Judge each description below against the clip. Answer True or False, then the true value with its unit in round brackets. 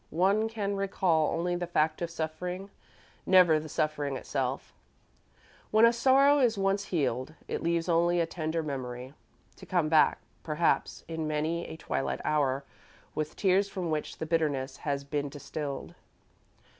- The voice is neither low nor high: True (160 Hz)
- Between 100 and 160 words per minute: True (150 wpm)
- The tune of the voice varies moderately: True (3.9 semitones)